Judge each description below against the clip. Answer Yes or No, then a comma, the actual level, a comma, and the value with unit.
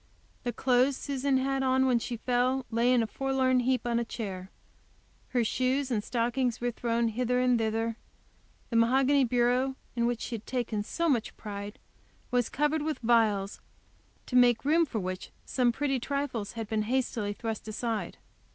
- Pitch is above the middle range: Yes, high, 245 Hz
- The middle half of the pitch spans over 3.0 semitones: No, narrow, 2.5 semitones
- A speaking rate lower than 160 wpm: No, average, 170 wpm